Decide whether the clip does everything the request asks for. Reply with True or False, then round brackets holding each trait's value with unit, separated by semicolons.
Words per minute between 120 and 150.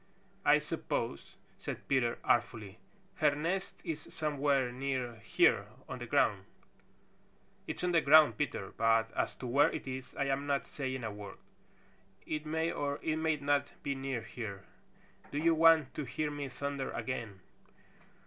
False (160 wpm)